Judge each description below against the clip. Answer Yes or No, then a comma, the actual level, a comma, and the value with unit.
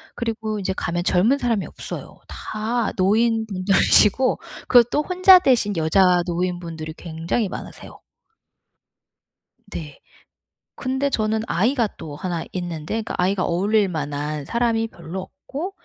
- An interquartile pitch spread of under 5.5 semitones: Yes, average, 5.1 semitones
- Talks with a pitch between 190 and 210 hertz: Yes, high, 200 Hz